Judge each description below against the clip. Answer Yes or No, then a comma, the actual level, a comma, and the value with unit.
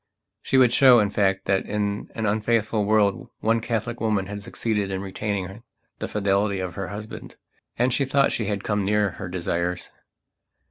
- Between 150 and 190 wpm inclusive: Yes, average, 175 wpm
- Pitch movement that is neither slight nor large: No, narrow, 2.2 semitones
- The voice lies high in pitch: No, low, 105 Hz